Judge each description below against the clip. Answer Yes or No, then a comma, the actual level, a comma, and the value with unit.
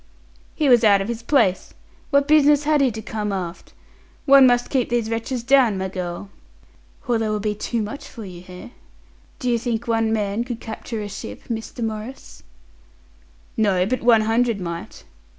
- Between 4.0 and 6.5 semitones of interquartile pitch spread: No, average, 3.1 semitones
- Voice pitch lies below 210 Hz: No, high, 225 Hz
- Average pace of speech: Yes, average, 180 wpm